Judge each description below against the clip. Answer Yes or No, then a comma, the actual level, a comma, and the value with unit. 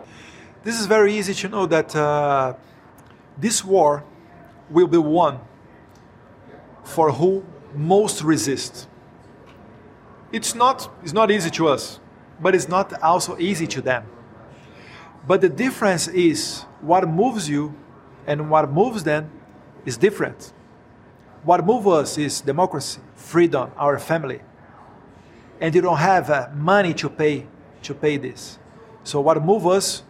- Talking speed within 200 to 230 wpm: No, slow, 135 wpm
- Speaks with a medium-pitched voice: Yes, medium, 160 Hz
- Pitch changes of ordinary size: Yes, average, 4.9 semitones